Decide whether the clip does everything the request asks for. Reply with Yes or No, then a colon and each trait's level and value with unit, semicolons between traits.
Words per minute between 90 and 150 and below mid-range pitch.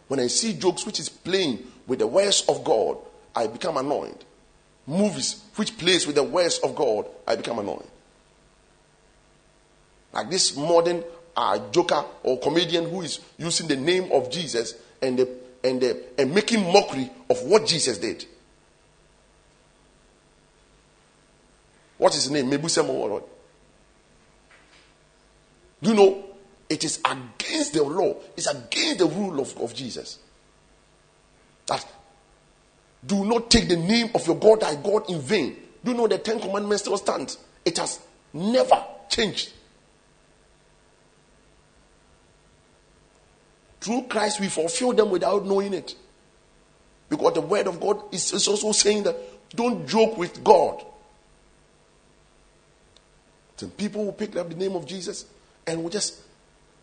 No: slow, 135 wpm; medium, 175 Hz